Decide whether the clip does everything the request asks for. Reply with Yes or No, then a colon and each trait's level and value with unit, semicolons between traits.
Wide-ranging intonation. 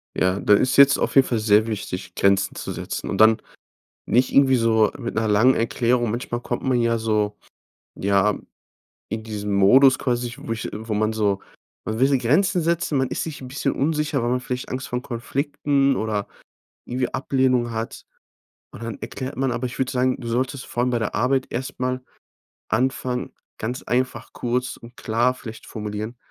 No: average, 2.9 semitones